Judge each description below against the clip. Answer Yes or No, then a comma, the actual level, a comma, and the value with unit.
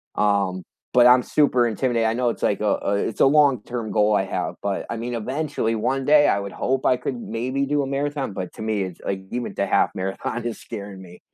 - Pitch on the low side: Yes, low, 115 Hz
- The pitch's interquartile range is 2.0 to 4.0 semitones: No, average, 4.7 semitones